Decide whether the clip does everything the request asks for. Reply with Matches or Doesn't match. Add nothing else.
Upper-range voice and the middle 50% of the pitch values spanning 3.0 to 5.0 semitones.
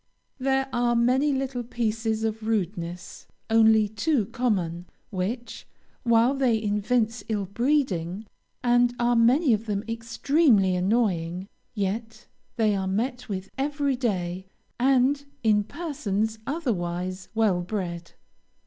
Matches